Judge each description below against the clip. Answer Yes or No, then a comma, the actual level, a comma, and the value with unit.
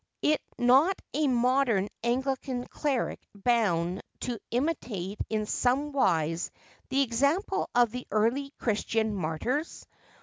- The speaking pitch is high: Yes, high, 245 Hz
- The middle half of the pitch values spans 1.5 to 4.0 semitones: No, average, 4.6 semitones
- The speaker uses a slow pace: Yes, slow, 105 wpm